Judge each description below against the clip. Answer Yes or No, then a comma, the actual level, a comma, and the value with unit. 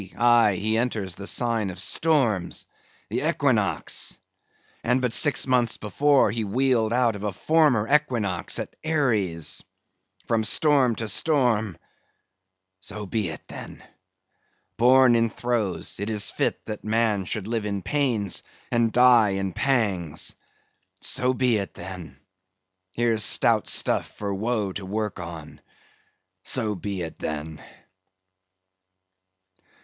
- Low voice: Yes, low, 110 Hz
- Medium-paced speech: No, slow, 125 wpm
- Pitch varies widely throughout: No, average, 4.0 semitones